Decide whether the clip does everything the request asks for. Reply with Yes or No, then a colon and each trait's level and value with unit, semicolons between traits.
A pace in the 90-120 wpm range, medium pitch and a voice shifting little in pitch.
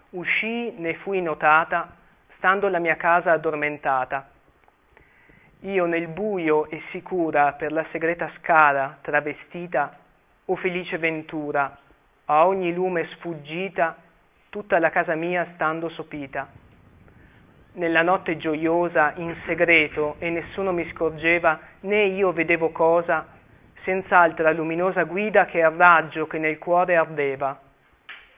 Yes: slow, 115 wpm; medium, 165 Hz; narrow, 2.3 semitones